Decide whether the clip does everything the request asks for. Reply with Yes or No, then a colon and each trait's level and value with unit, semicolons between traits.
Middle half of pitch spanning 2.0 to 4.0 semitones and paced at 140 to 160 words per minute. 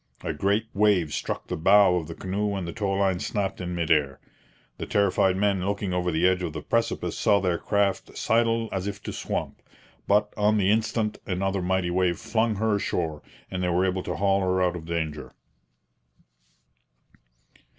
No: narrow, 2.4 semitones; average, 185 wpm